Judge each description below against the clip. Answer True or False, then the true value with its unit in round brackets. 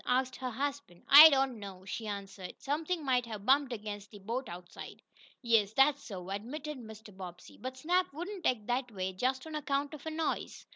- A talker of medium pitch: False (250 Hz)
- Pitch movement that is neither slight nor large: False (5.7 semitones)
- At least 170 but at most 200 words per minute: True (190 wpm)